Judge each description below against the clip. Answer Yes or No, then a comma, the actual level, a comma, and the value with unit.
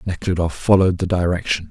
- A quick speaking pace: No, average, 140 wpm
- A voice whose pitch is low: Yes, very low, 90 Hz